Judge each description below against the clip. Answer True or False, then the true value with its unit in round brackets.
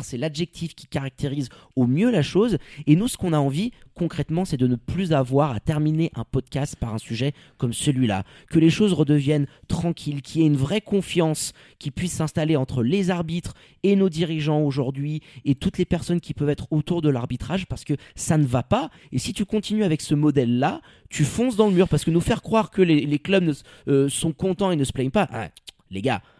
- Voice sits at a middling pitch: True (150 Hz)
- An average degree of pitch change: True (4.0 semitones)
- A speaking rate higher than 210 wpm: True (220 wpm)